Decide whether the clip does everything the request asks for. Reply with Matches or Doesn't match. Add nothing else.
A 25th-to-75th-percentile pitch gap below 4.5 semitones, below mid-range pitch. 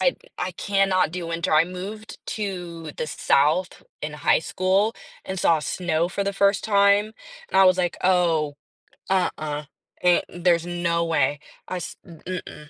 Doesn't match